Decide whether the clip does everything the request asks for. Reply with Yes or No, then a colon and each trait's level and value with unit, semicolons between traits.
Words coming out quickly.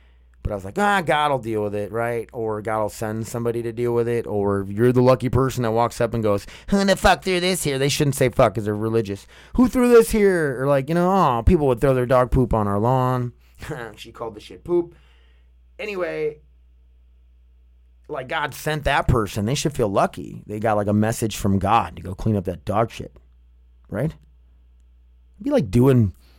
Yes: fast, 215 wpm